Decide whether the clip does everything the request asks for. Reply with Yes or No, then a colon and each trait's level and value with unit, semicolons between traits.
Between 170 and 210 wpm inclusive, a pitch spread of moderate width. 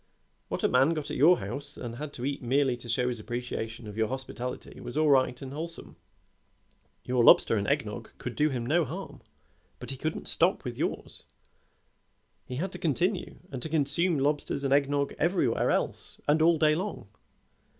Yes: average, 190 wpm; average, 4.0 semitones